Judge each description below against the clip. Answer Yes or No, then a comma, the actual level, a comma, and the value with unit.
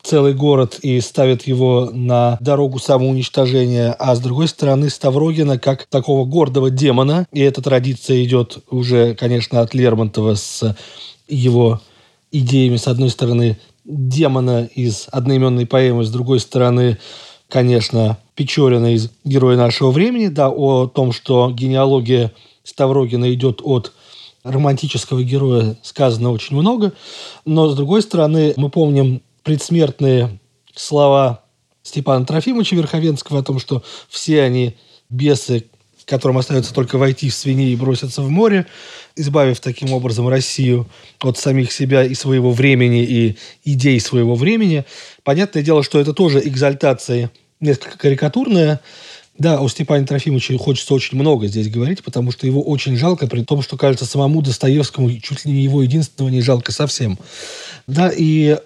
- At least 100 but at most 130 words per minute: No, average, 140 wpm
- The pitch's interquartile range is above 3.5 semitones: No, average, 2.7 semitones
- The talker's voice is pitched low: Yes, low, 130 Hz